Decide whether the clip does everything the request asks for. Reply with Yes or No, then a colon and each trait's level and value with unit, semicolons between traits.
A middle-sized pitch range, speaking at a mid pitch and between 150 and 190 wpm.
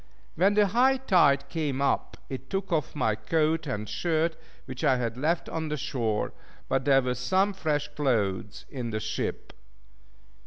Yes: average, 4.8 semitones; medium, 145 Hz; average, 165 wpm